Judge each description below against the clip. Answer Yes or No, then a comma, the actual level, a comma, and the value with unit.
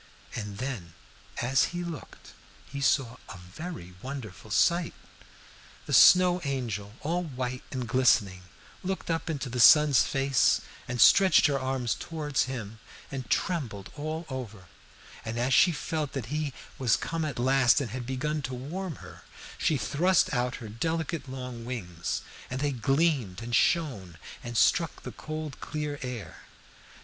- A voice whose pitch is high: No, low, 130 Hz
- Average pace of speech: Yes, average, 150 wpm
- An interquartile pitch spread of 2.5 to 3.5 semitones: No, average, 4.5 semitones